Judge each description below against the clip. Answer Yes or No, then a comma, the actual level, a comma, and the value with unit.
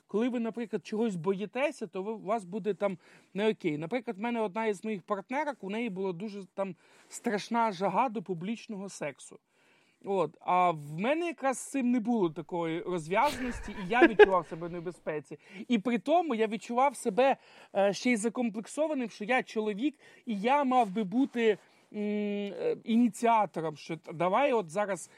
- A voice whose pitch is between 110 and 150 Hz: No, high, 220 Hz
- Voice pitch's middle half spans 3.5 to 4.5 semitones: Yes, average, 3.8 semitones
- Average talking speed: No, fast, 160 wpm